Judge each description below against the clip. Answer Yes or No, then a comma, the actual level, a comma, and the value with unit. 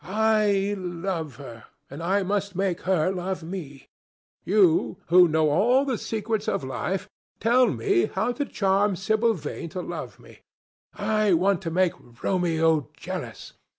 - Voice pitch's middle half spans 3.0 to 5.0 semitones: Yes, average, 4.1 semitones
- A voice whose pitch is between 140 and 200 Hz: Yes, high, 190 Hz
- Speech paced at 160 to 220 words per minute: No, average, 150 wpm